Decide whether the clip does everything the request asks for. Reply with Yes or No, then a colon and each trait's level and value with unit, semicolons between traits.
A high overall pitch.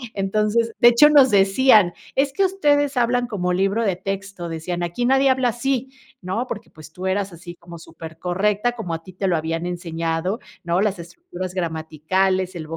Yes: high, 195 Hz